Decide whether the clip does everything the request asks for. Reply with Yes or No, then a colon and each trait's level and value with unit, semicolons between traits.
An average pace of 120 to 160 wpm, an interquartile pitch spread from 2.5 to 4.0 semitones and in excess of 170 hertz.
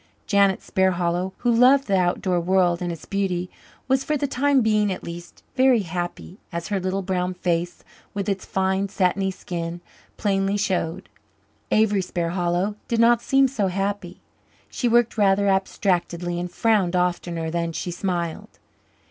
Yes: average, 150 wpm; average, 2.8 semitones; high, 190 Hz